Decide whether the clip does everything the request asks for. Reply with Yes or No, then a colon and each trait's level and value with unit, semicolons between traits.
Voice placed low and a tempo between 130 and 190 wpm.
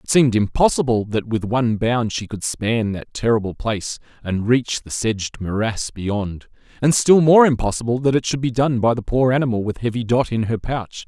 No: low, 115 Hz; fast, 205 wpm